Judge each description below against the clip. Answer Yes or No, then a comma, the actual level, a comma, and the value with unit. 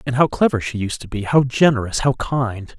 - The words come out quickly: Yes, fast, 235 wpm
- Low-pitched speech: Yes, low, 120 Hz